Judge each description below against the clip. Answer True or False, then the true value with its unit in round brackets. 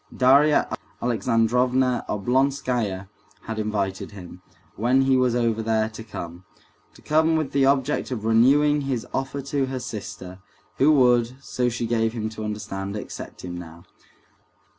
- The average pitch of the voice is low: True (120 Hz)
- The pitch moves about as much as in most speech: True (3.8 semitones)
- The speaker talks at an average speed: True (145 wpm)